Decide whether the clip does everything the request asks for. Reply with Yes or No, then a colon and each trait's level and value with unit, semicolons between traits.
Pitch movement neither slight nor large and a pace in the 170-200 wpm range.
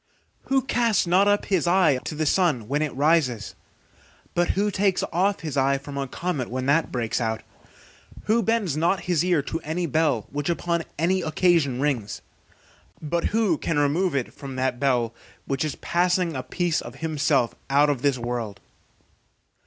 Yes: average, 4.7 semitones; average, 175 wpm